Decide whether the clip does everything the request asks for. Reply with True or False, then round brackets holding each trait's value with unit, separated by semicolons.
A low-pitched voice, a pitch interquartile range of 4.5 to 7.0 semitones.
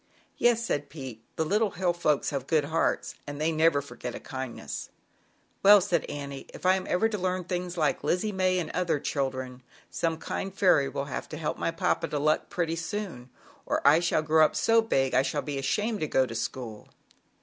False (160 Hz; 4.8 semitones)